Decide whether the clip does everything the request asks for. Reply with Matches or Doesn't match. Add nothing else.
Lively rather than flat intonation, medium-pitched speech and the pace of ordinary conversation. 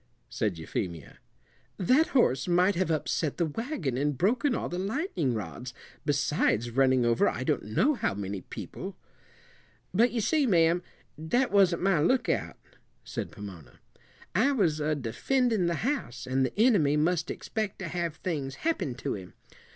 Matches